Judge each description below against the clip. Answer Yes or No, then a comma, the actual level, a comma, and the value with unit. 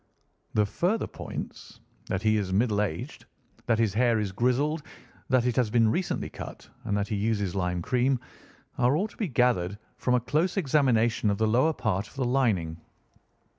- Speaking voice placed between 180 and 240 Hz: No, low, 115 Hz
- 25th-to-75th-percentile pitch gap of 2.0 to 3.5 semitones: No, average, 4.0 semitones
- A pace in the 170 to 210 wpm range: Yes, average, 180 wpm